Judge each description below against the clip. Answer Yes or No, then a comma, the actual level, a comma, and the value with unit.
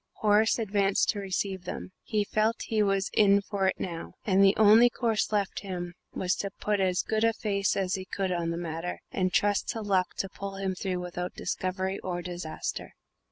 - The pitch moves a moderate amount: No, narrow, 2.1 semitones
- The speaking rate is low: No, average, 200 wpm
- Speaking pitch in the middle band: No, high, 195 Hz